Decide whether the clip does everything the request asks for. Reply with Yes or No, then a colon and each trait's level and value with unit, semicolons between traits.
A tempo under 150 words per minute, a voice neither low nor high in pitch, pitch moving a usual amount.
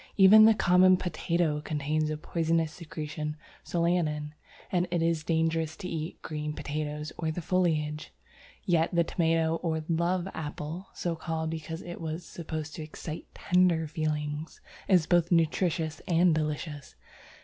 No: average, 140 wpm; medium, 160 Hz; narrow, 2.0 semitones